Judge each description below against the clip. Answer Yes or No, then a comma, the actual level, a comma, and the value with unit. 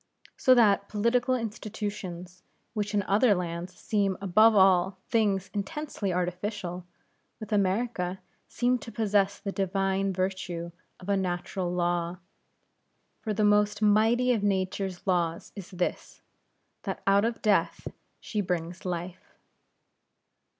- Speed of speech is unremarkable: No, slow, 120 wpm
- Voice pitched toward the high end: Yes, high, 195 Hz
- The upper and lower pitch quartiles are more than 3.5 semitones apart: No, average, 2.7 semitones